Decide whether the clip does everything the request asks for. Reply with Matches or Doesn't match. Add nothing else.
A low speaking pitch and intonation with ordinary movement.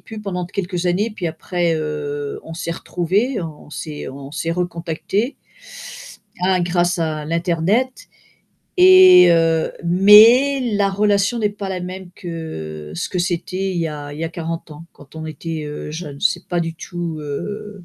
Doesn't match